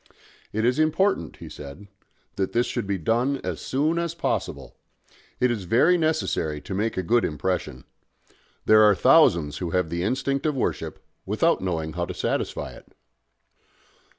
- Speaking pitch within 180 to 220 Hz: No, low, 110 Hz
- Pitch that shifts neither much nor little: No, wide, 7.9 semitones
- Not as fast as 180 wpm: Yes, average, 160 wpm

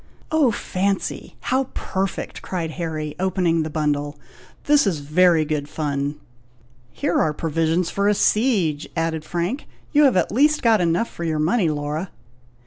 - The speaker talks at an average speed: Yes, average, 150 wpm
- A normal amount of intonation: Yes, average, 4.5 semitones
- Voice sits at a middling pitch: Yes, medium, 170 Hz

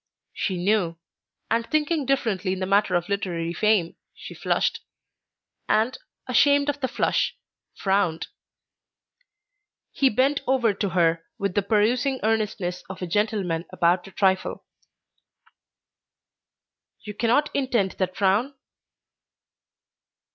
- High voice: Yes, high, 205 Hz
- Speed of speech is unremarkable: No, slow, 115 wpm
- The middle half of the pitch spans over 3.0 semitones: Yes, average, 4.9 semitones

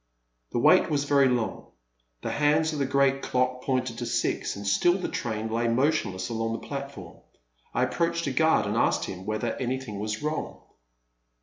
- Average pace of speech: Yes, average, 180 wpm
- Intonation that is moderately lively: Yes, average, 4.1 semitones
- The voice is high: No, low, 130 Hz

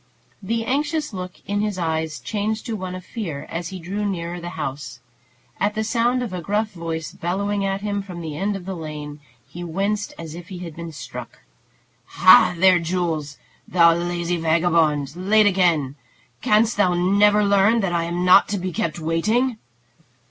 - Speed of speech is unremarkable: Yes, average, 180 wpm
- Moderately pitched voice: Yes, medium, 180 Hz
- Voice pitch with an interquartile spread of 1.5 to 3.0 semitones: No, average, 3.6 semitones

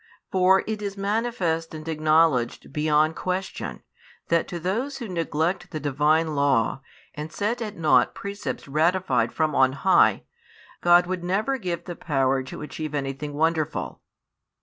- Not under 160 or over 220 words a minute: No, average, 150 wpm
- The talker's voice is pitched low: No, medium, 165 Hz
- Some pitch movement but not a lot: Yes, average, 3.9 semitones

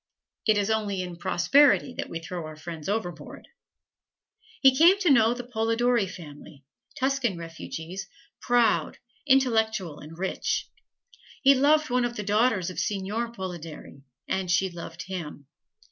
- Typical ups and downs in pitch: No, wide, 5.9 semitones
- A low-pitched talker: No, high, 205 Hz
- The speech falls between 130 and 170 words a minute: Yes, average, 140 wpm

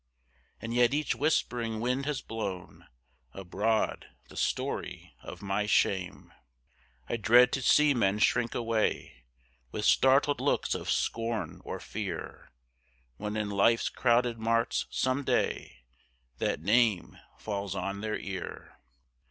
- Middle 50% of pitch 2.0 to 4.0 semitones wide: Yes, average, 3.6 semitones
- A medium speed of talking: No, slow, 125 wpm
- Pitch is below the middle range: Yes, low, 115 Hz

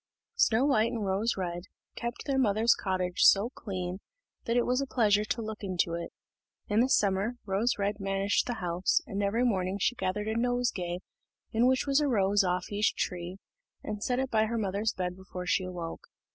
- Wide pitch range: No, average, 3.9 semitones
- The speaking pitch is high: Yes, high, 205 Hz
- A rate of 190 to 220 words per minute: Yes, average, 195 wpm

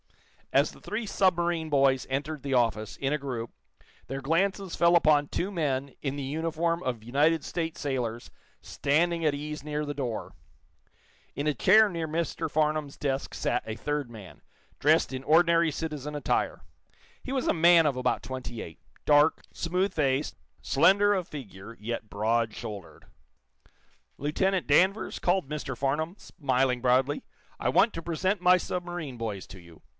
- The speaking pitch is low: No, medium, 150 Hz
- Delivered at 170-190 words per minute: No, average, 160 wpm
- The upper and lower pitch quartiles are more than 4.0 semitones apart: Yes, average, 4.5 semitones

